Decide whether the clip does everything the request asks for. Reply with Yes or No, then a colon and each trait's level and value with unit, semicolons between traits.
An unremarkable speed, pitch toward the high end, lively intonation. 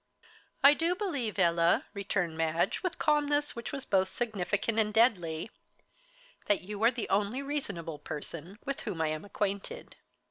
Yes: average, 150 wpm; high, 205 Hz; wide, 7.8 semitones